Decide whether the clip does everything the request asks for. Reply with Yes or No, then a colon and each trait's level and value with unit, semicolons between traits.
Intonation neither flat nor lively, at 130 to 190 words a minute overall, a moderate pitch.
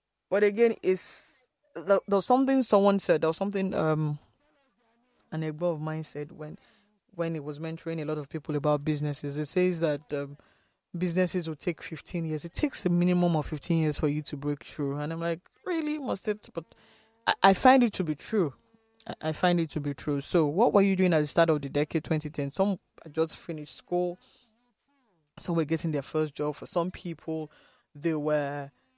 No: average, 4.5 semitones; average, 200 wpm; medium, 165 Hz